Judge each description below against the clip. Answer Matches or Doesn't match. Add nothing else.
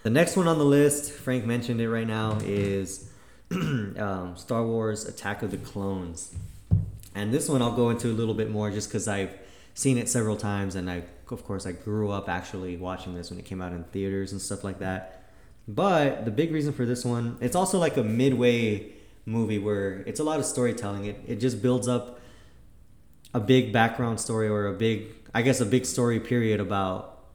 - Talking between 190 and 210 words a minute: Matches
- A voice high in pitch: Doesn't match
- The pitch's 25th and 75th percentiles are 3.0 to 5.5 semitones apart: Matches